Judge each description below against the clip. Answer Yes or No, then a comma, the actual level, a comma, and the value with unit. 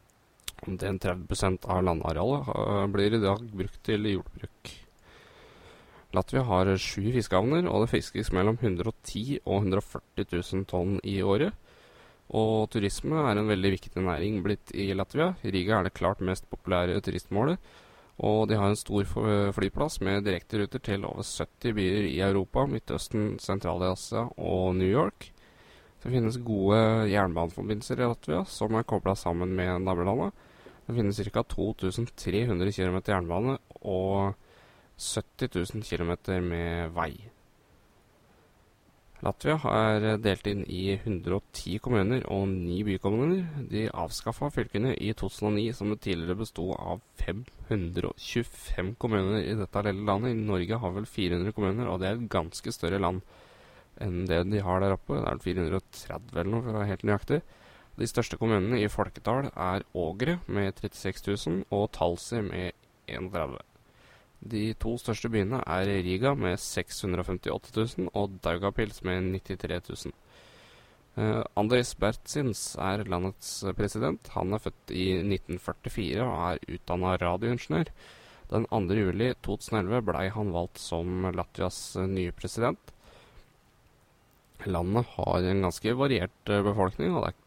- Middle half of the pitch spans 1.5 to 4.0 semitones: Yes, average, 3.1 semitones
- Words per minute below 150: Yes, average, 140 wpm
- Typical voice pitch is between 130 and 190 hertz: No, low, 100 Hz